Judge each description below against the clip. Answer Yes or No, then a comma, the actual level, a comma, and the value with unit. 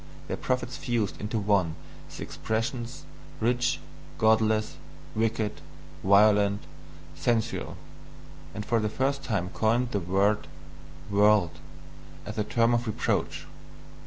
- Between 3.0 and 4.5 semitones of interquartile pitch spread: No, narrow, 2.6 semitones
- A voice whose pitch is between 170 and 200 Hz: No, low, 110 Hz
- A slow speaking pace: Yes, slow, 110 wpm